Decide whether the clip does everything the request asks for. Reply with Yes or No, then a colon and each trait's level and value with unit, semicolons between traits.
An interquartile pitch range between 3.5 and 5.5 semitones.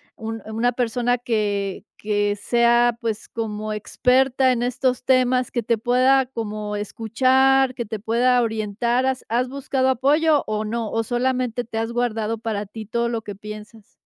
No: average, 2.8 semitones